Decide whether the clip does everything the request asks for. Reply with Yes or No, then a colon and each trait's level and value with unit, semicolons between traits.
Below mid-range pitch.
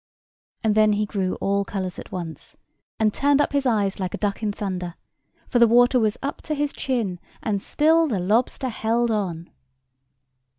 No: high, 215 Hz